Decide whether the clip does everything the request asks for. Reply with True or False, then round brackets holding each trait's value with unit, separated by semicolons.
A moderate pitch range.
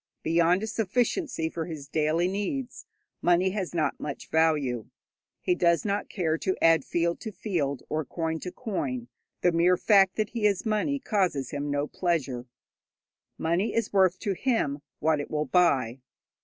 True (4.5 semitones)